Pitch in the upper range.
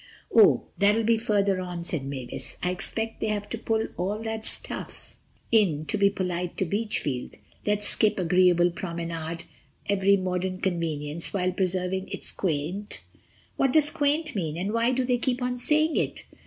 Yes: high, 195 Hz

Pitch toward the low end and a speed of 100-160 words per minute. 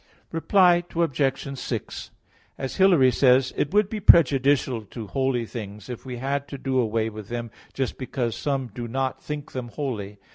No: low, 130 Hz; average, 180 wpm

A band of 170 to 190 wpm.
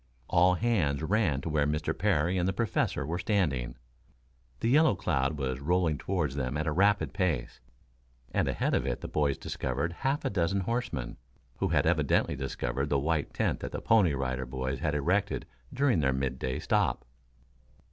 Yes: average, 175 wpm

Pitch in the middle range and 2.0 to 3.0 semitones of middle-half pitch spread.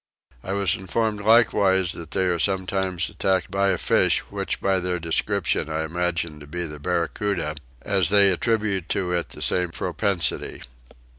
No: very low, 95 Hz; narrow, 2.6 semitones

